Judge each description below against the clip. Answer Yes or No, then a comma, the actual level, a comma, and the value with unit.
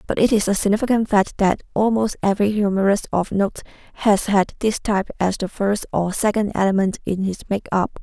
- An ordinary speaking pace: Yes, average, 185 wpm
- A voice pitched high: Yes, high, 200 Hz